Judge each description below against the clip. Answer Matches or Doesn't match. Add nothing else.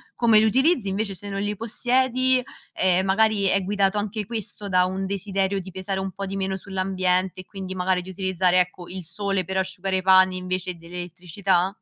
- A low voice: Doesn't match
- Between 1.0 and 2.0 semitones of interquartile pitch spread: Matches